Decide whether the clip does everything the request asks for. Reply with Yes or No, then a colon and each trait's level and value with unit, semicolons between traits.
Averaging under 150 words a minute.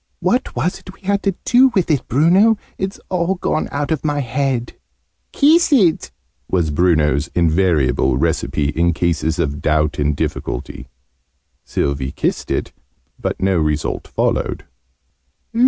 Yes: average, 140 wpm